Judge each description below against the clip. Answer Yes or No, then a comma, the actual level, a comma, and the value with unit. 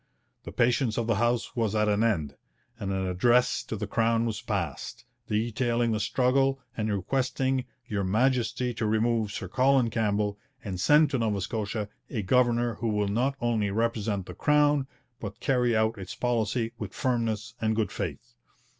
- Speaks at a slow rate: No, average, 170 wpm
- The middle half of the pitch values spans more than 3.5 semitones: No, average, 2.7 semitones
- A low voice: Yes, low, 115 Hz